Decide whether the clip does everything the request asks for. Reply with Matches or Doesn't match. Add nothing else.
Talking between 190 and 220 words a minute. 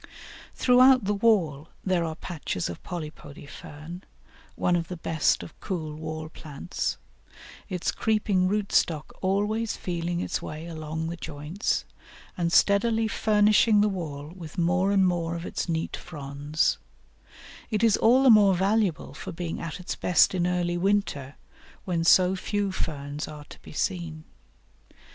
Doesn't match